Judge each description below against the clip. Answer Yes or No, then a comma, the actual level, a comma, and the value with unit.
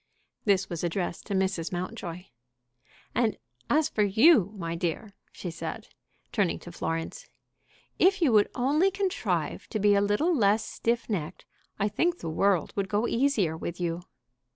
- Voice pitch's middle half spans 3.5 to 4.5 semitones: No, wide, 5.5 semitones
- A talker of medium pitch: No, high, 200 Hz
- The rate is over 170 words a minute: No, average, 155 wpm